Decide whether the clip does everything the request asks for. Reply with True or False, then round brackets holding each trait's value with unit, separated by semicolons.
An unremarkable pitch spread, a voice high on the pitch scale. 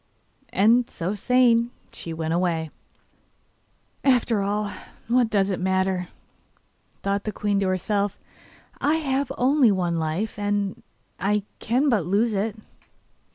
True (3.8 semitones; 205 Hz)